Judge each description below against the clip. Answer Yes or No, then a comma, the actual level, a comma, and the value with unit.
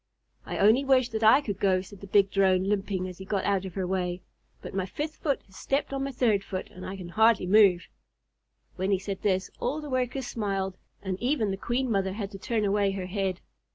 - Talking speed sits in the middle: No, fast, 230 wpm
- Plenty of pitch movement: No, average, 3.4 semitones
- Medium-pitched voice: No, high, 200 Hz